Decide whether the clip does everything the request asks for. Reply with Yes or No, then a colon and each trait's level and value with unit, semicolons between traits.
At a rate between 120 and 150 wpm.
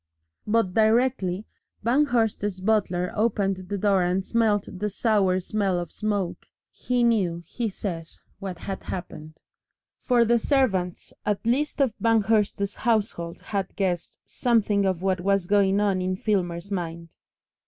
Yes: average, 140 wpm